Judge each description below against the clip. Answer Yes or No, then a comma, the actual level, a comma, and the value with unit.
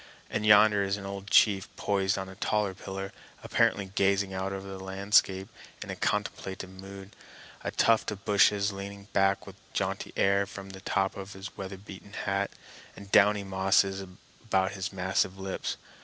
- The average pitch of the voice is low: Yes, very low, 95 Hz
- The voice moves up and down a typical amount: No, narrow, 0.7 semitones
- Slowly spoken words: No, average, 165 wpm